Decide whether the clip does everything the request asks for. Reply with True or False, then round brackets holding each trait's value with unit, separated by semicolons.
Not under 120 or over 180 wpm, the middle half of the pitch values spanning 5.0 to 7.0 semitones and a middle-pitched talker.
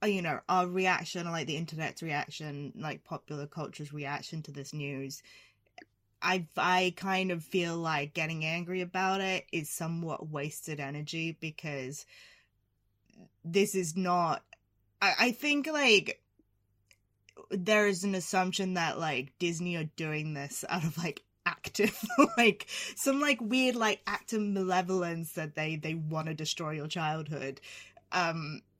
False (140 wpm; 4.0 semitones; 165 Hz)